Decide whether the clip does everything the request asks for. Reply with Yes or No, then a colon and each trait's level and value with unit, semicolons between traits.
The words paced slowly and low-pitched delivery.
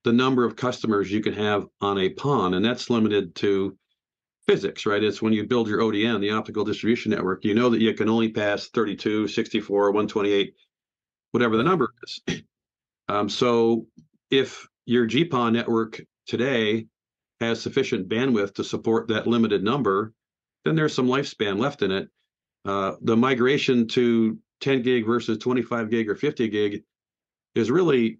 No: average, 160 wpm; low, 115 Hz